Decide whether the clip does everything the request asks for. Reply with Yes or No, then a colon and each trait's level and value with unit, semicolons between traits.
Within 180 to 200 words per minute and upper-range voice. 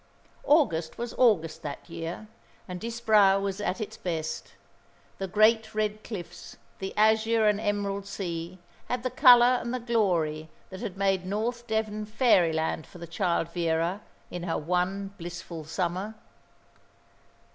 No: average, 140 wpm; high, 195 Hz